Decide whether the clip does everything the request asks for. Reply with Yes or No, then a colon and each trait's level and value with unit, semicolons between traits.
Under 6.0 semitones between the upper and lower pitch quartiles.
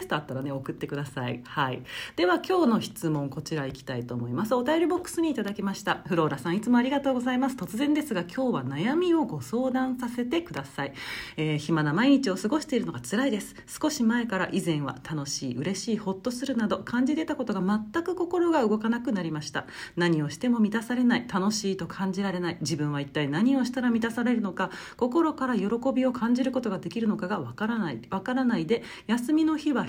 No: wide, 8.0 semitones